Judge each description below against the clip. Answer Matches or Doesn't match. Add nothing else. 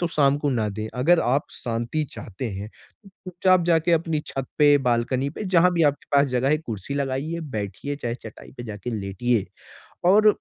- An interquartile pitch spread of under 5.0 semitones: Doesn't match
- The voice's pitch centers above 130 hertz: Matches